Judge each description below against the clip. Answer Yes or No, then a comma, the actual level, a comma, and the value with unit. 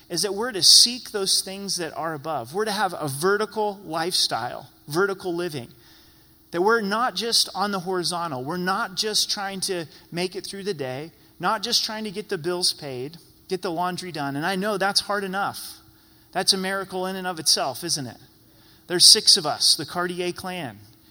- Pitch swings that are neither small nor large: Yes, average, 3.2 semitones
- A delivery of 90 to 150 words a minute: No, average, 195 wpm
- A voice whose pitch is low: No, medium, 185 Hz